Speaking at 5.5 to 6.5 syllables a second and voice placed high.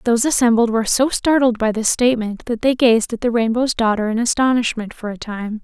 Yes: 5.8 syllables/s; high, 230 Hz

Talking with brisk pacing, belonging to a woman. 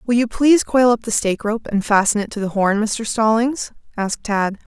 Yes: fast, 225 wpm; female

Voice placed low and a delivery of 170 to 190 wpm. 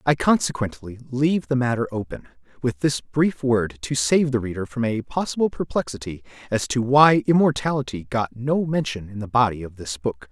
Yes: low, 125 Hz; average, 180 wpm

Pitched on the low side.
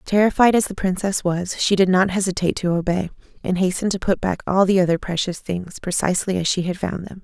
No: medium, 185 Hz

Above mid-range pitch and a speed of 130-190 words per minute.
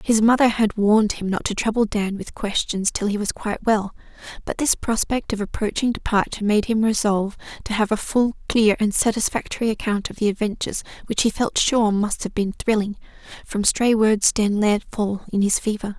No: high, 215 Hz; average, 200 wpm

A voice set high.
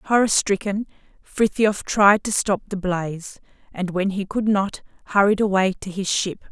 Yes: high, 195 Hz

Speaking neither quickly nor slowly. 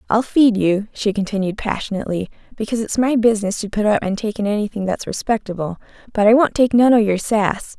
No: fast, 210 wpm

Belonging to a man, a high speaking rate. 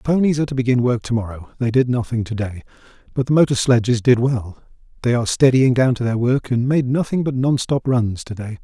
Yes: male; fast, 230 wpm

